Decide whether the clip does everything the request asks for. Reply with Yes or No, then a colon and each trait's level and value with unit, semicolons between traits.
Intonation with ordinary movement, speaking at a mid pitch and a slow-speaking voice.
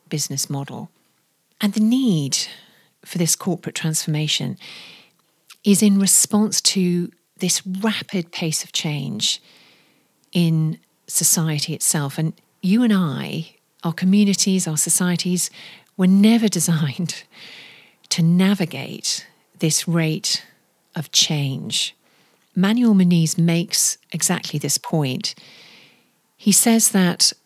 Yes: average, 3.5 semitones; medium, 175 Hz; slow, 105 wpm